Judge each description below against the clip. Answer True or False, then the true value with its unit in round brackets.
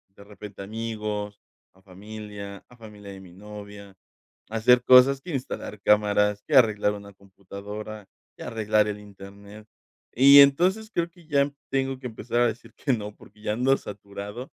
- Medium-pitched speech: False (105 Hz)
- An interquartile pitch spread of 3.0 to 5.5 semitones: True (3.4 semitones)